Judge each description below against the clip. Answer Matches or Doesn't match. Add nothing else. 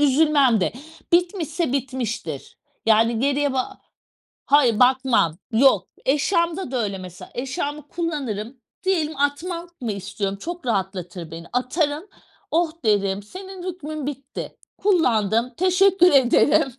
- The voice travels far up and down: Matches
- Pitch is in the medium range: Doesn't match